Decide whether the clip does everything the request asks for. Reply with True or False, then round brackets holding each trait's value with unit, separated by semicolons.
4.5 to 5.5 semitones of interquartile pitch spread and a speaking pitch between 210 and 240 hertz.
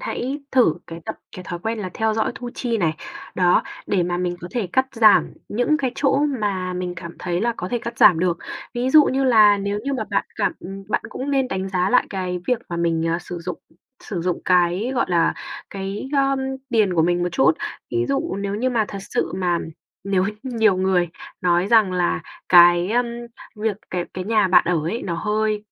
False (4.8 semitones; 195 Hz)